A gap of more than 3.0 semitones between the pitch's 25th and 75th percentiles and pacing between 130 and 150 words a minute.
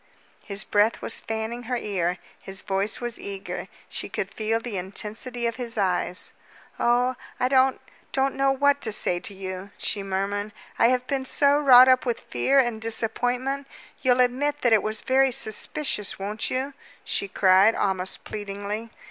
No: average, 4.2 semitones; average, 165 wpm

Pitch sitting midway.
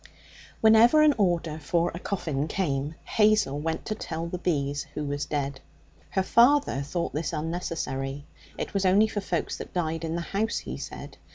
Yes: medium, 165 Hz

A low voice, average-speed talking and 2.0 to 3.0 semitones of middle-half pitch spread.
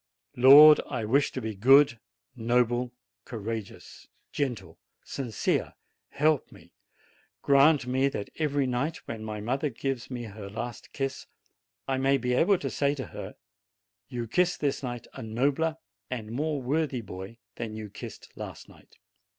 No: low, 125 Hz; average, 150 wpm; average, 3.6 semitones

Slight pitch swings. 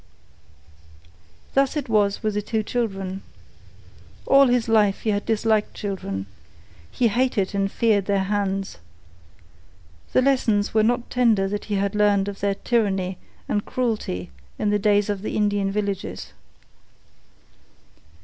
Yes: narrow, 2.3 semitones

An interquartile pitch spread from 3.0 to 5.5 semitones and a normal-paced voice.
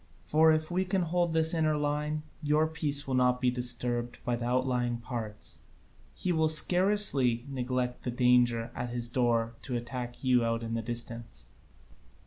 Yes: average, 4.3 semitones; average, 165 wpm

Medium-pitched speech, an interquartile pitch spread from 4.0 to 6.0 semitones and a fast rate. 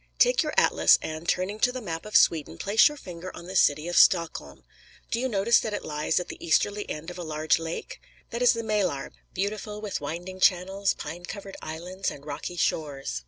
Yes: medium, 180 Hz; average, 4.5 semitones; fast, 210 wpm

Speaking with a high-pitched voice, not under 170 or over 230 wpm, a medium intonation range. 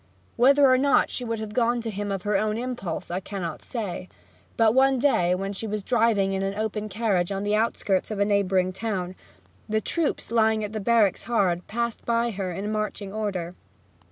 Yes: high, 210 Hz; average, 200 wpm; average, 3.0 semitones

